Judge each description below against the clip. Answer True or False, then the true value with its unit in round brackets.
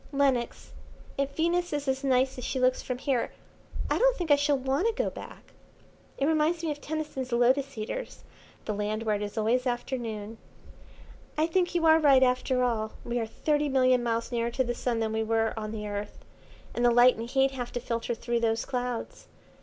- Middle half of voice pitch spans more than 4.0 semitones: False (3.5 semitones)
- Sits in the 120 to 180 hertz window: False (255 Hz)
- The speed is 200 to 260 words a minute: True (205 wpm)